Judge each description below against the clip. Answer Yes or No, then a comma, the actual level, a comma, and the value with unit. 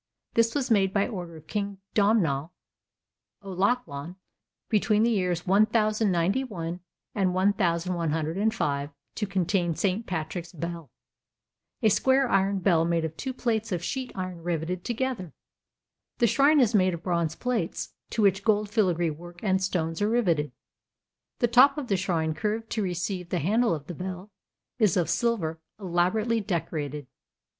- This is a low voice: No, high, 190 Hz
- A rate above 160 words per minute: No, average, 145 wpm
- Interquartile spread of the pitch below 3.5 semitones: No, average, 4.4 semitones